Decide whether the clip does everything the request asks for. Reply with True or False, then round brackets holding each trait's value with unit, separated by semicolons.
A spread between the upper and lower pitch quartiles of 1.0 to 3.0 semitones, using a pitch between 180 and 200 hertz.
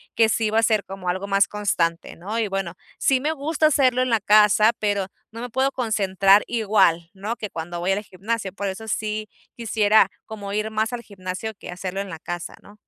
False (2.7 semitones; 210 Hz)